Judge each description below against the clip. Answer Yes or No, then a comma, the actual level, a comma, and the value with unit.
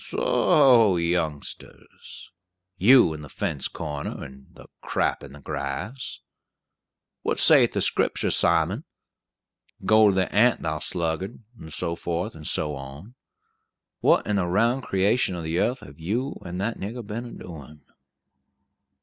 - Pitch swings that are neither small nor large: No, wide, 6.0 semitones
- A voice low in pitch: Yes, very low, 90 Hz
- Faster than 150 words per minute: No, average, 145 wpm